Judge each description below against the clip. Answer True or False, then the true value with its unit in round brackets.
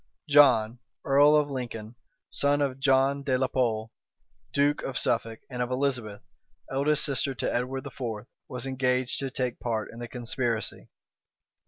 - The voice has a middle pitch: False (130 Hz)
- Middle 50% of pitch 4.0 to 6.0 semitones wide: False (2.6 semitones)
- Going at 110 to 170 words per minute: True (150 wpm)